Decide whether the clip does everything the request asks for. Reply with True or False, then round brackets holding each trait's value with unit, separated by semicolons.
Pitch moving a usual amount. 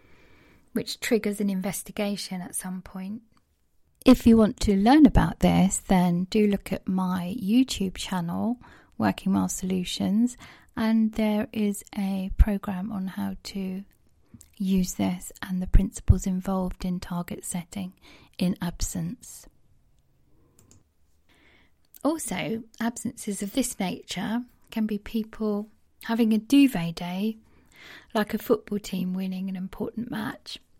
True (3.0 semitones)